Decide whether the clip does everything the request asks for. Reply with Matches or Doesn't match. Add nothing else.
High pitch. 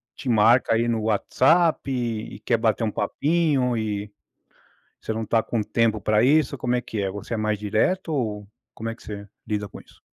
Doesn't match